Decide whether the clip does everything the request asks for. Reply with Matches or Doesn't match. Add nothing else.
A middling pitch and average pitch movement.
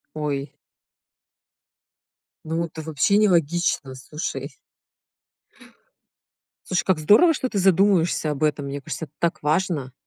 Matches